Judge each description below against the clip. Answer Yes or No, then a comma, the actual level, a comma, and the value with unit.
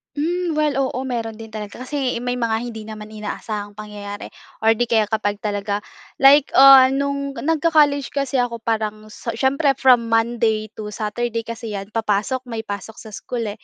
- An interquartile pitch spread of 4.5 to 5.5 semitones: No, average, 3.7 semitones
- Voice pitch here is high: Yes, high, 230 Hz